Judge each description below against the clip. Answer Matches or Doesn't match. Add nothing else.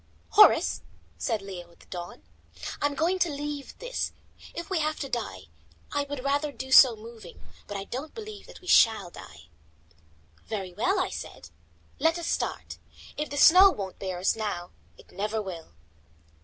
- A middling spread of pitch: Doesn't match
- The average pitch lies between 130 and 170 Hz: Doesn't match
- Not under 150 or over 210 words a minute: Matches